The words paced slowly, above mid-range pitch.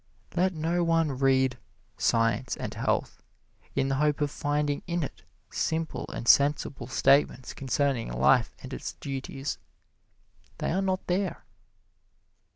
No: slow, 130 wpm; medium, 140 Hz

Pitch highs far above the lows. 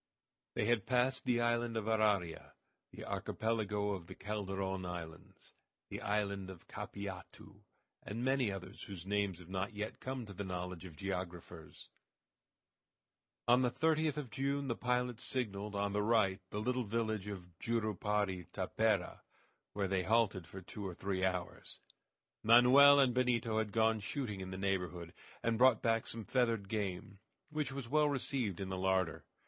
No: average, 3.9 semitones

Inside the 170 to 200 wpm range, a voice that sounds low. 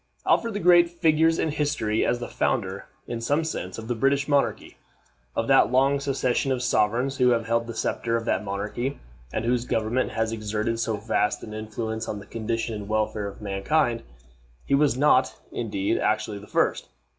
Yes: average, 185 wpm; low, 115 Hz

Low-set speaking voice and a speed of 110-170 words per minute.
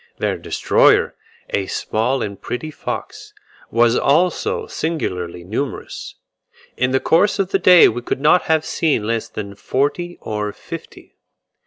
Yes: low, 130 Hz; average, 140 wpm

